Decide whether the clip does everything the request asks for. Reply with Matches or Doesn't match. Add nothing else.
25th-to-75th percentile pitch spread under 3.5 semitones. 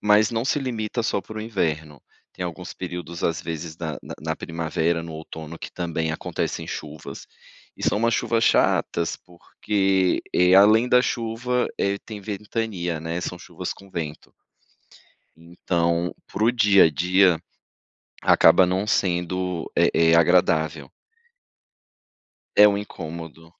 Doesn't match